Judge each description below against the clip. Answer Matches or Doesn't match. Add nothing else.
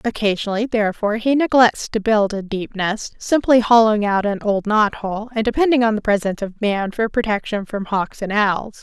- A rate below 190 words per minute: Doesn't match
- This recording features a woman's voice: Matches